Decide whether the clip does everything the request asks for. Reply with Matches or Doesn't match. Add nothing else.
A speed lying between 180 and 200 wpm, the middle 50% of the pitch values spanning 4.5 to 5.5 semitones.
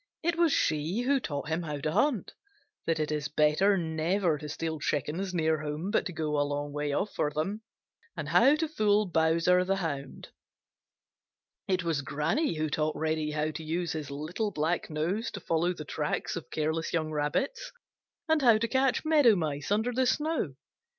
Matches